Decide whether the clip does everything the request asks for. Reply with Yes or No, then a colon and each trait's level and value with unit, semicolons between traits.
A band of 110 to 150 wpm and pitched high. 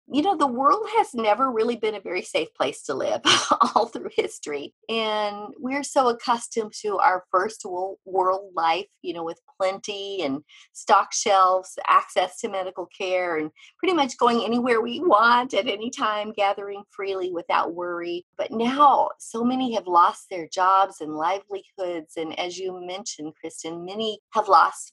No: average, 165 wpm; high, 205 Hz